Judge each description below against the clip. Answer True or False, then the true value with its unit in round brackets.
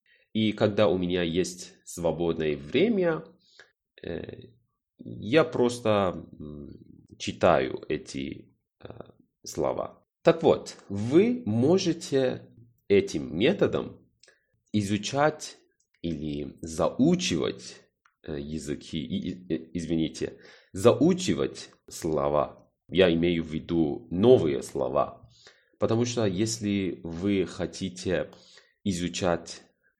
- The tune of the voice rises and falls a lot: True (5.8 semitones)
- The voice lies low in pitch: True (95 Hz)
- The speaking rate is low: True (75 wpm)